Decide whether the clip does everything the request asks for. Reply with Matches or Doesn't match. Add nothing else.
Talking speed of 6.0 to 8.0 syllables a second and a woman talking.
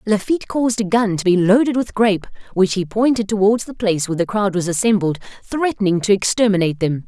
Matches